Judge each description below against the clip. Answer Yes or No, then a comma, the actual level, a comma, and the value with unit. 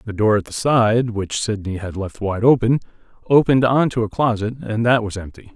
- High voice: No, low, 110 Hz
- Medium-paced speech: No, fast, 215 wpm